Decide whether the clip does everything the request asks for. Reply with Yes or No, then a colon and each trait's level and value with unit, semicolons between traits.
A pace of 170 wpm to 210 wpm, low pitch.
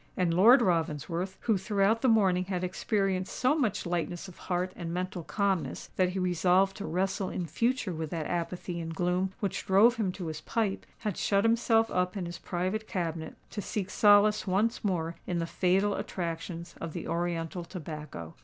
No: average, 175 wpm; medium, 185 Hz